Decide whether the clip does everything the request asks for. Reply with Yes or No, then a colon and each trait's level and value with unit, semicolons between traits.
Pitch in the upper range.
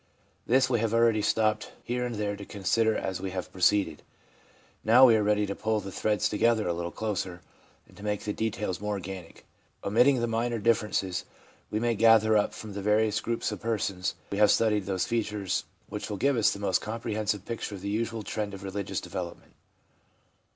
No: low, 105 Hz